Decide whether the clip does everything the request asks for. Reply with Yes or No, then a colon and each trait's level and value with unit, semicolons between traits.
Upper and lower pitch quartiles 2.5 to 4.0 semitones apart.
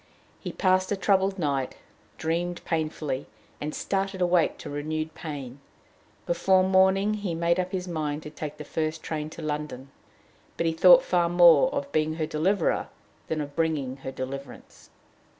Yes: average, 3.5 semitones